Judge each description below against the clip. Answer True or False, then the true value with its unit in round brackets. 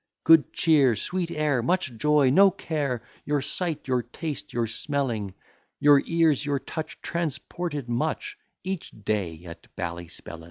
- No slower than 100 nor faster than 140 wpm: True (135 wpm)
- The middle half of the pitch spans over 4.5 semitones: True (5.5 semitones)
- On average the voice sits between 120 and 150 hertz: True (140 Hz)